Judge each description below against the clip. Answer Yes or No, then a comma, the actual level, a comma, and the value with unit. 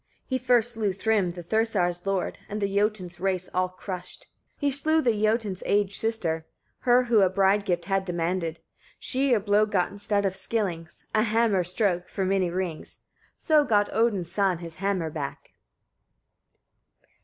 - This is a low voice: No, high, 195 Hz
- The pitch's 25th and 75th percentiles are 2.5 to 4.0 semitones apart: Yes, average, 3.6 semitones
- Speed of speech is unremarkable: Yes, average, 165 wpm